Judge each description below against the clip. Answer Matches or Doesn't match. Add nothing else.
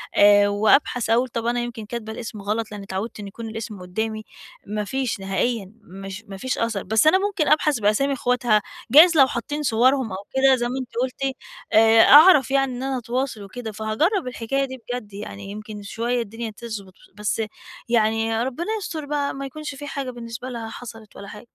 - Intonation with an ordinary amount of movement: Matches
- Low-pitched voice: Doesn't match